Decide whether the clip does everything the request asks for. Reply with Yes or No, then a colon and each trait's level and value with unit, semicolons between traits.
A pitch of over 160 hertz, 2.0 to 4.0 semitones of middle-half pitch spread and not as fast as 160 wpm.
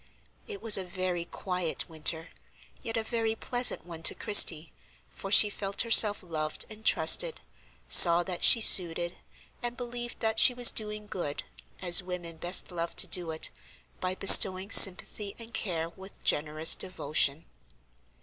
No: medium, 185 Hz; average, 4.5 semitones; average, 150 wpm